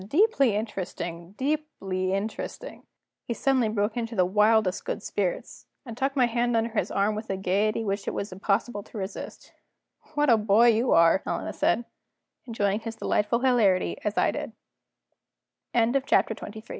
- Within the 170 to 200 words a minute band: No, average, 155 wpm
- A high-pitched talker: Yes, high, 220 Hz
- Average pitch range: Yes, average, 3.3 semitones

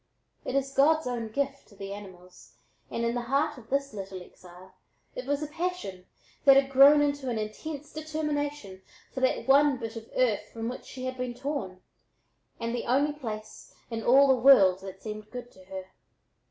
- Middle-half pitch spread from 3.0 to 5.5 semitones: Yes, average, 4.8 semitones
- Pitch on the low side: No, very high, 250 Hz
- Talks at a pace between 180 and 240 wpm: Yes, average, 190 wpm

